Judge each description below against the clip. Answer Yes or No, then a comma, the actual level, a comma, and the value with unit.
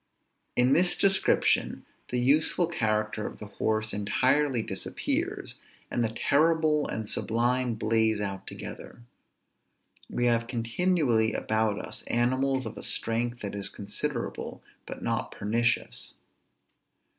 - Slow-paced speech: Yes, slow, 120 wpm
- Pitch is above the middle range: No, low, 120 Hz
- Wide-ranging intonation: No, average, 3.7 semitones